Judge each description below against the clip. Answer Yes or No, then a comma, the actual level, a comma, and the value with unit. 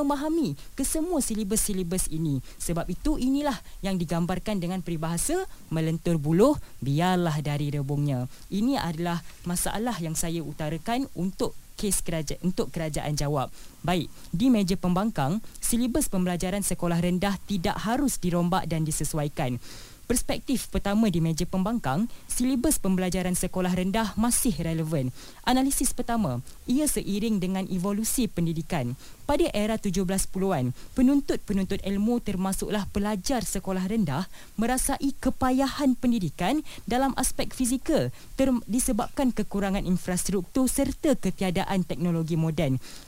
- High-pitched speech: Yes, high, 195 Hz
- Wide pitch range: Yes, wide, 6.1 semitones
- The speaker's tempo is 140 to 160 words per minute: No, average, 115 wpm